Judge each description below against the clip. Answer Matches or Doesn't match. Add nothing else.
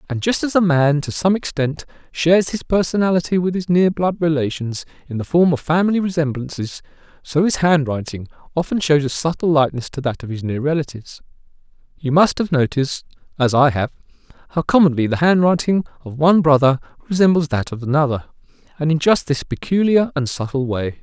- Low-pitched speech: Doesn't match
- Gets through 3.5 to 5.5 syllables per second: Doesn't match